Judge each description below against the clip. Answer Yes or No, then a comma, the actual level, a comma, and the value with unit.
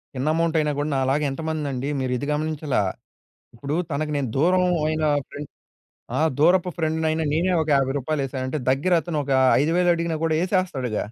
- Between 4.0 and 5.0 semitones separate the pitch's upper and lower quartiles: No, average, 3.0 semitones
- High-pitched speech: No, medium, 155 Hz